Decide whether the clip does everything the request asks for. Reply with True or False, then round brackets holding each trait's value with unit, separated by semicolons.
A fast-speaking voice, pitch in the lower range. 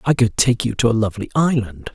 True (245 wpm; 115 Hz)